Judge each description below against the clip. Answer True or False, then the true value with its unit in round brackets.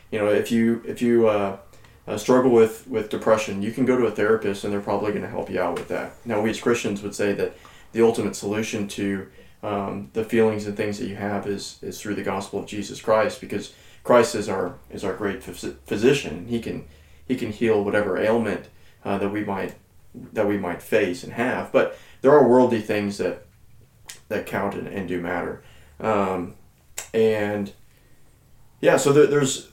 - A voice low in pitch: True (105 Hz)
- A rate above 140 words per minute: True (200 wpm)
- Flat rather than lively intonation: True (2.3 semitones)